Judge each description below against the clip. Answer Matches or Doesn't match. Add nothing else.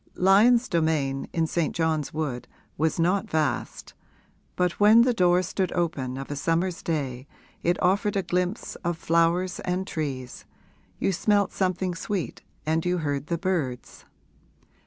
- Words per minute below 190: Matches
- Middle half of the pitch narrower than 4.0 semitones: Matches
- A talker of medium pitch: Matches